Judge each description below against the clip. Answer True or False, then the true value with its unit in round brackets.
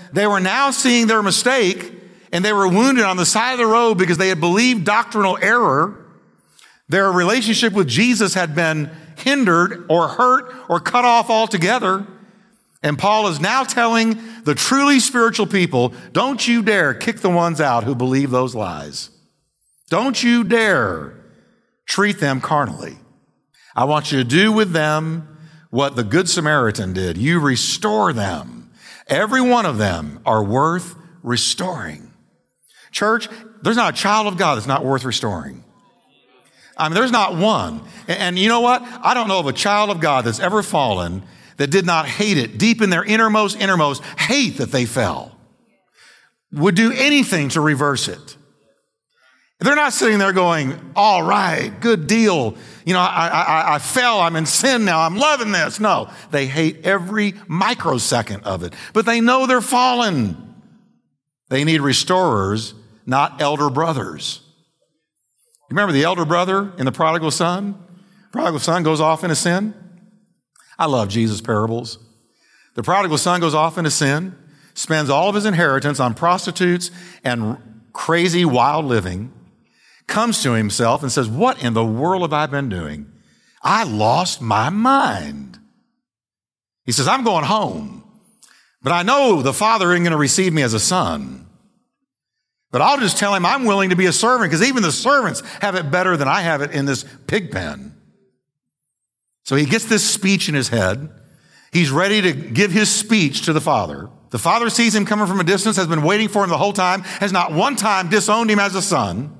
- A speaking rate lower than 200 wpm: True (170 wpm)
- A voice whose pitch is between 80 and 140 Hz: False (180 Hz)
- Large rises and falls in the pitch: True (7.3 semitones)